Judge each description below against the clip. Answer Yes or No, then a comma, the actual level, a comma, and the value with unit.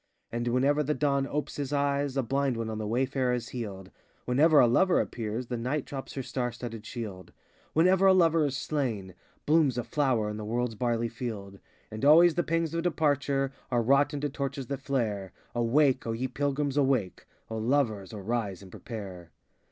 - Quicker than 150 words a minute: Yes, average, 185 wpm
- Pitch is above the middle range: No, low, 130 Hz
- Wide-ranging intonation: No, average, 4.0 semitones